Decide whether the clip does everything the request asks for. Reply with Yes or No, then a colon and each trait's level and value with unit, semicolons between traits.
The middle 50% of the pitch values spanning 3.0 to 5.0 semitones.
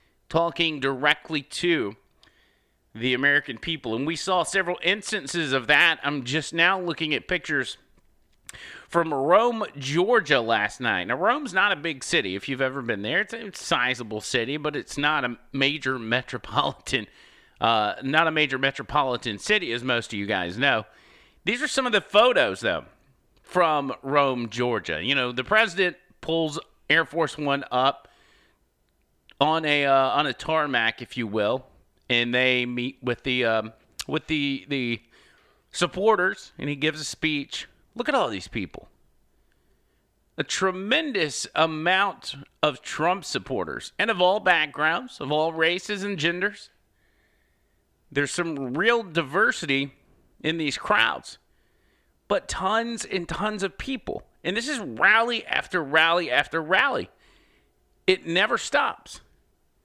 No: wide, 5.5 semitones